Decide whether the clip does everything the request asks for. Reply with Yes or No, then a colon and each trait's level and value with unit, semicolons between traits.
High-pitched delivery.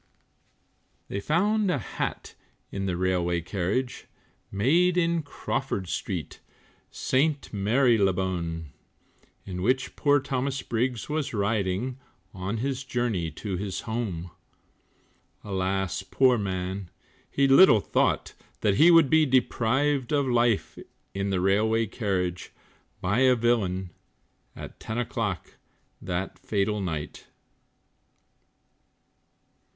No: low, 110 Hz